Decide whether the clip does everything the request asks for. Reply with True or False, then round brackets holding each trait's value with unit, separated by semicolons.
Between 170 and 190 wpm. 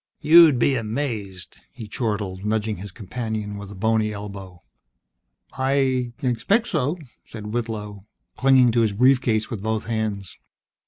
False (145 wpm)